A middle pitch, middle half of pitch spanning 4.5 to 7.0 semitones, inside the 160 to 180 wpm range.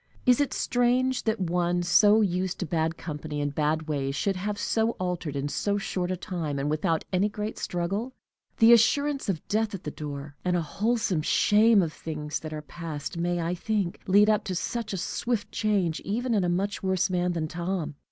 No: medium, 180 Hz; average, 4.8 semitones; average, 200 wpm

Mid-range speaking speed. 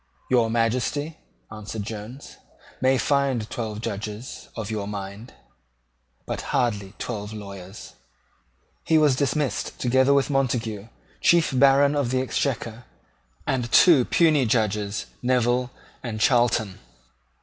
No: slow, 115 wpm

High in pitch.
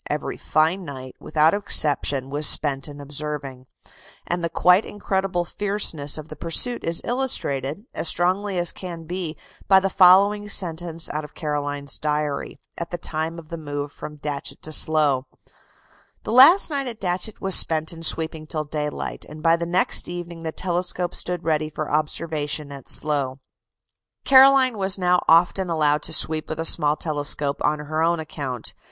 No: medium, 160 Hz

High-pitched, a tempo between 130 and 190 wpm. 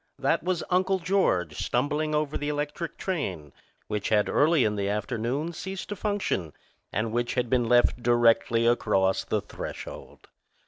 No: low, 125 Hz; average, 150 wpm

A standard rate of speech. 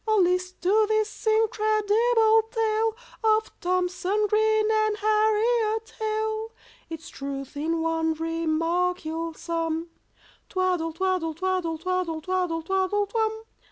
No: slow, 115 wpm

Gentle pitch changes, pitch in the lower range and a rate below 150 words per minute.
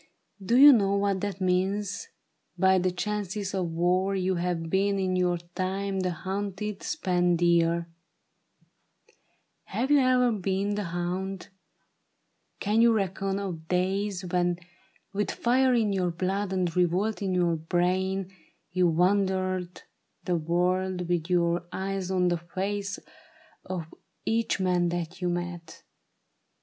No: narrow, 2.1 semitones; medium, 185 Hz; slow, 135 wpm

